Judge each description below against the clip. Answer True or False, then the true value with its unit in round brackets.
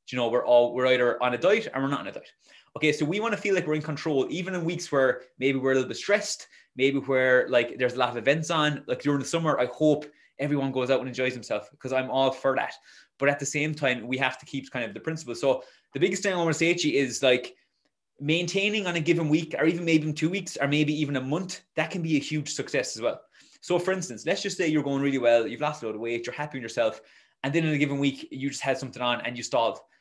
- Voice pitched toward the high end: False (140 Hz)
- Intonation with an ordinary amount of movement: True (3.7 semitones)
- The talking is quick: True (290 wpm)